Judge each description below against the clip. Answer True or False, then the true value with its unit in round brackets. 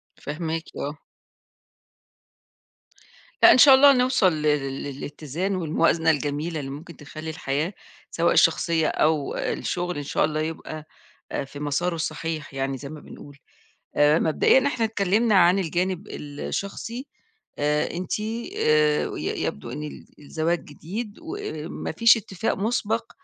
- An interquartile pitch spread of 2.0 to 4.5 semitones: False (5.0 semitones)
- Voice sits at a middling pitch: True (160 Hz)